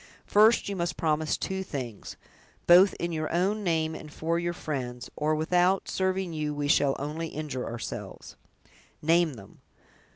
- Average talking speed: Yes, average, 155 wpm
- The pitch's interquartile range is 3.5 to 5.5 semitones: No, average, 3.0 semitones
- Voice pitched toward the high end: No, medium, 160 Hz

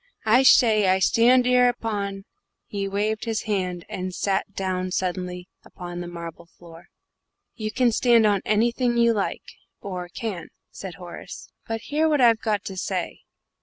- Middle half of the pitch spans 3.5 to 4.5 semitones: Yes, average, 4.0 semitones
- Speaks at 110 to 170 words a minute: Yes, average, 165 wpm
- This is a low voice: No, high, 200 Hz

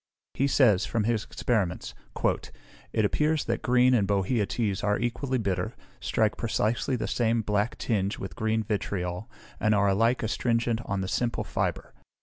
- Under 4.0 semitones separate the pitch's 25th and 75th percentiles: Yes, average, 2.8 semitones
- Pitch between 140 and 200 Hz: No, low, 110 Hz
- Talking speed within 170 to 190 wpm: No, average, 155 wpm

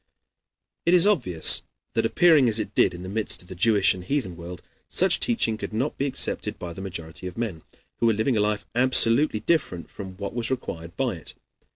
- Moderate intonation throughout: No, wide, 6.0 semitones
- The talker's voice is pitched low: Yes, low, 110 Hz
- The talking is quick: Yes, fast, 210 wpm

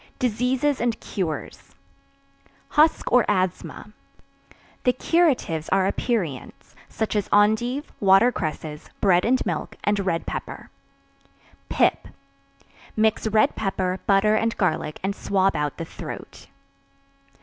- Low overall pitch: No, high, 205 Hz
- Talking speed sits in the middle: No, slow, 115 wpm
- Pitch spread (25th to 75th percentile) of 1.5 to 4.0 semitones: No, average, 4.5 semitones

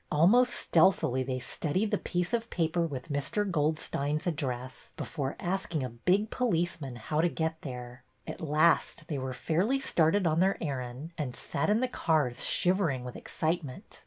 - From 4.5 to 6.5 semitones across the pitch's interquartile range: Yes, average, 5.0 semitones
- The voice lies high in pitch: No, medium, 160 Hz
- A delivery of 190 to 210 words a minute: No, average, 170 wpm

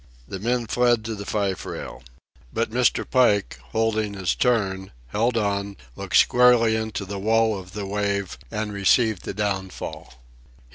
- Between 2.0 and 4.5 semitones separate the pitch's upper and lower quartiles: Yes, narrow, 2.4 semitones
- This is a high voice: No, low, 105 Hz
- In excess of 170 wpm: No, average, 150 wpm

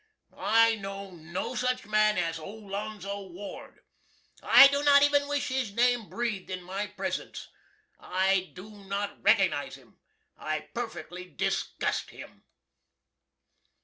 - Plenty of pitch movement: No, average, 3.7 semitones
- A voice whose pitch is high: Yes, high, 205 Hz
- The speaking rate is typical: No, slow, 120 wpm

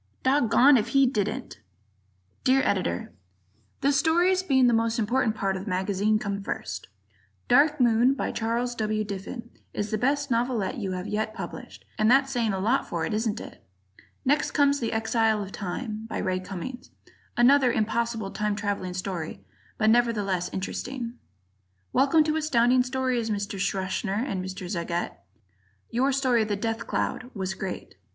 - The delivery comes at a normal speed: Yes, average, 160 wpm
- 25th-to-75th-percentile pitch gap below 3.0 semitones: No, average, 4.3 semitones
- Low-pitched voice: No, high, 225 Hz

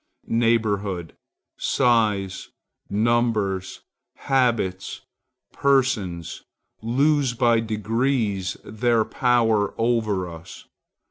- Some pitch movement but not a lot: Yes, average, 3.5 semitones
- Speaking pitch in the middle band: No, low, 110 Hz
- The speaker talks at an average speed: No, slow, 65 wpm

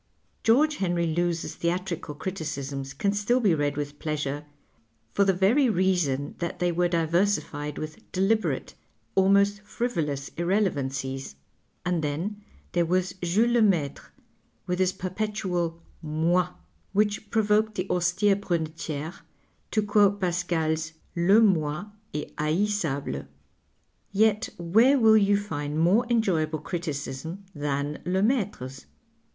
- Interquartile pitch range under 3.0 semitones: No, average, 4.8 semitones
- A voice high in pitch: No, medium, 175 Hz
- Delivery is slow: Yes, slow, 120 wpm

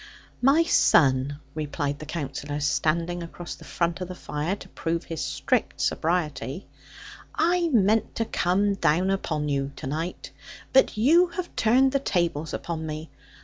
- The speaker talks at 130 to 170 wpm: Yes, average, 150 wpm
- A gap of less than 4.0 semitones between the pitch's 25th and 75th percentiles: No, wide, 5.5 semitones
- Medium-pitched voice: Yes, medium, 170 Hz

